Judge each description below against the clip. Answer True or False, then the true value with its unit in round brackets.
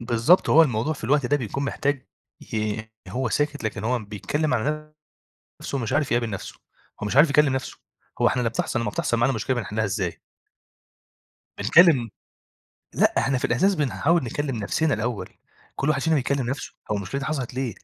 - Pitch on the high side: False (130 Hz)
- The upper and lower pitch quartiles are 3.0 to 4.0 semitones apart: False (4.4 semitones)